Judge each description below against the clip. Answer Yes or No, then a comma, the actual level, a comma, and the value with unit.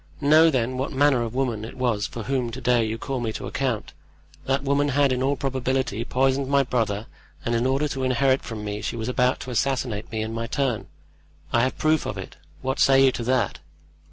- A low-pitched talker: Yes, low, 130 Hz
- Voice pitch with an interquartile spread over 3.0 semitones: No, average, 2.7 semitones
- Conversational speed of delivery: No, fast, 220 wpm